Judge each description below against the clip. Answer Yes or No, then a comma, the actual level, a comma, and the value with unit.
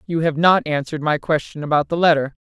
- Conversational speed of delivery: No, fast, 220 wpm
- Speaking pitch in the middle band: Yes, medium, 155 Hz